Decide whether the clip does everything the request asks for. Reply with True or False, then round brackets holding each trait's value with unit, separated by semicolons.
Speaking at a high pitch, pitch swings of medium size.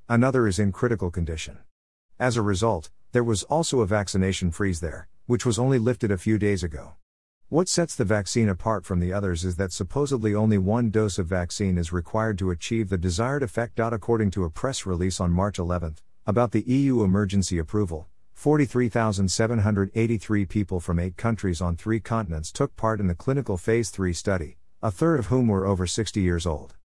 False (100 Hz; 4.3 semitones)